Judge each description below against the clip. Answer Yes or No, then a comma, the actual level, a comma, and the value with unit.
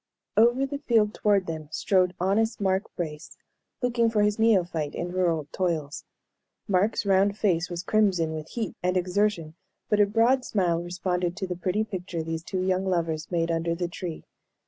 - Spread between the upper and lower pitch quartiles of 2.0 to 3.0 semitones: No, average, 3.6 semitones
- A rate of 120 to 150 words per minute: No, average, 170 wpm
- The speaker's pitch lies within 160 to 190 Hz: Yes, medium, 185 Hz